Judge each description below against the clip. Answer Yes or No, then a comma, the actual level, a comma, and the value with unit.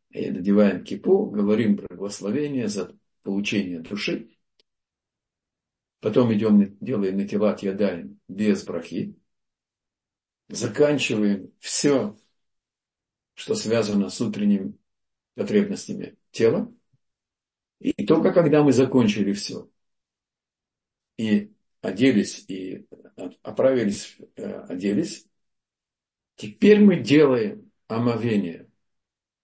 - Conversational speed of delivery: No, slow, 80 wpm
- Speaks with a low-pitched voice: Yes, low, 115 Hz